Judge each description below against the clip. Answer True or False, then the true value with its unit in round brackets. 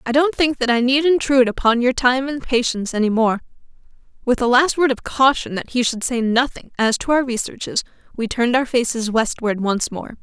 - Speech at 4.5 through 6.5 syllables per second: True (5.5 syllables/s)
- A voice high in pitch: True (250 Hz)